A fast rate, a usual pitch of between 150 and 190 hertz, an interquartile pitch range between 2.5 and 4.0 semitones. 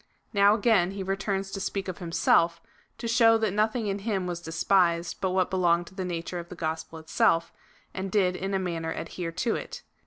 Yes: fast, 210 wpm; medium, 185 Hz; average, 2.8 semitones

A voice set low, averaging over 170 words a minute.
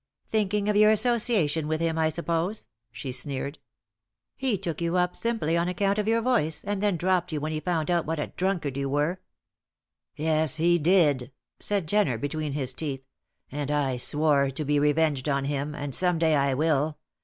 No: medium, 160 Hz; average, 190 wpm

